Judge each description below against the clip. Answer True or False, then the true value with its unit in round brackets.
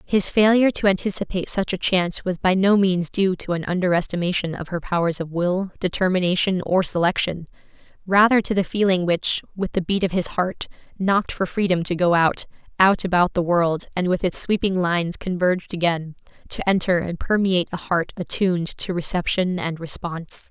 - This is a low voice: False (180 Hz)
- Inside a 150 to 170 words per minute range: False (185 wpm)